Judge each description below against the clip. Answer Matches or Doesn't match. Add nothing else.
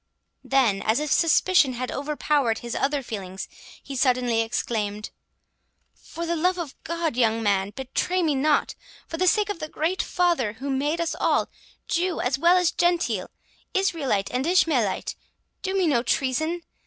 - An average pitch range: Doesn't match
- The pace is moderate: Matches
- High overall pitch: Matches